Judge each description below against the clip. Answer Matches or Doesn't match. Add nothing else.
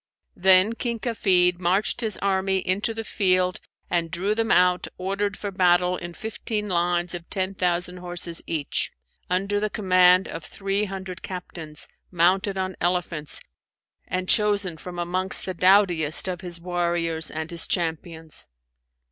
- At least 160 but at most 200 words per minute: Doesn't match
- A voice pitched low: Doesn't match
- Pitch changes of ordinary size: Doesn't match